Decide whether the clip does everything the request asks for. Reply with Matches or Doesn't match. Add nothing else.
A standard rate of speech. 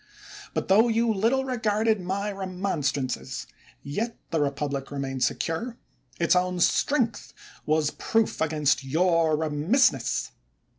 Doesn't match